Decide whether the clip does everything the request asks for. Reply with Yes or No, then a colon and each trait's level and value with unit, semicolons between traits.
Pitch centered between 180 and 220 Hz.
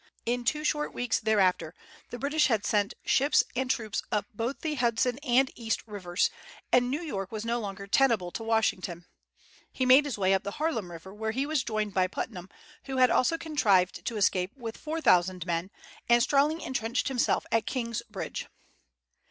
No: high, 230 Hz